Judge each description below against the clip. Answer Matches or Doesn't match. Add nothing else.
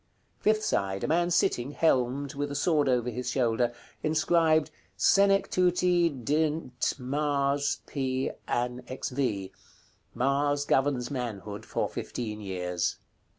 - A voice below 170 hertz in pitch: Matches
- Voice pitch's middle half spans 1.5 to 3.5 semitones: Doesn't match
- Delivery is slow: Matches